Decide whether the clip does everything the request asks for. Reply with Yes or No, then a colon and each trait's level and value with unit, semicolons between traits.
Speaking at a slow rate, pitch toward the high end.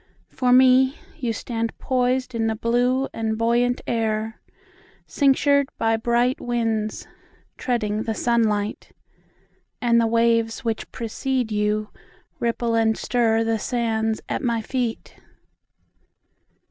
Yes: slow, 90 wpm; high, 230 Hz